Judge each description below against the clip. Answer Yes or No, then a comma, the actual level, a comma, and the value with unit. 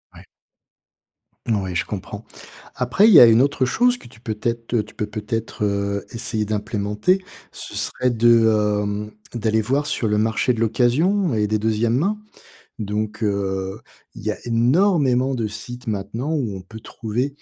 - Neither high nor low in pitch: No, low, 115 Hz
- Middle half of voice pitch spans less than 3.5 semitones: Yes, average, 3.1 semitones